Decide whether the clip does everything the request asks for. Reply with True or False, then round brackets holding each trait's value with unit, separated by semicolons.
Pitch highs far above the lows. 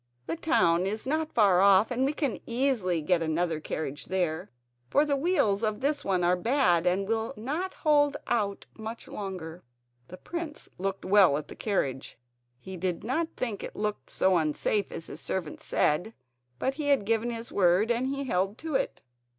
True (6.7 semitones)